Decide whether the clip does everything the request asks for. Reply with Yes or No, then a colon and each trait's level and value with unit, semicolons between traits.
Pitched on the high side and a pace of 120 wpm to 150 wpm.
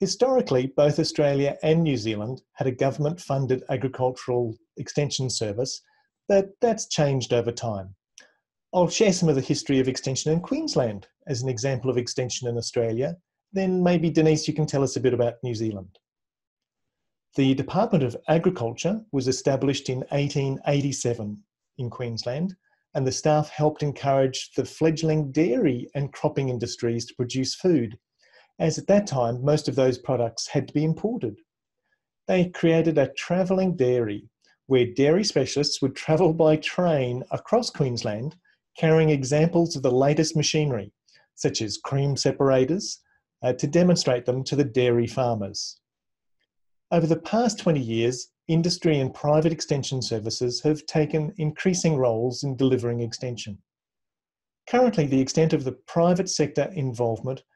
No: medium, 140 Hz; average, 145 wpm